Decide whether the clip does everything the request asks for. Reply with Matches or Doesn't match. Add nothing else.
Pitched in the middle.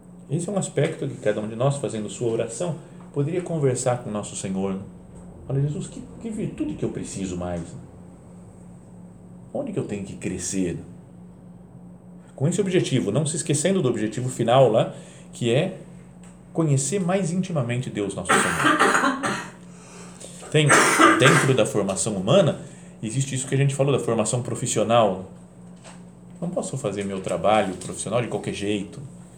Doesn't match